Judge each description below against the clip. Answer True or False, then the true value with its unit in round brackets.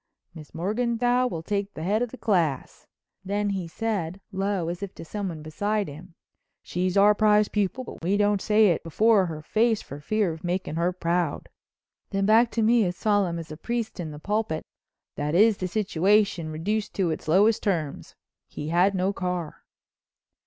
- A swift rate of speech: False (180 wpm)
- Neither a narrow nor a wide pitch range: True (4.0 semitones)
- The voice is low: False (195 Hz)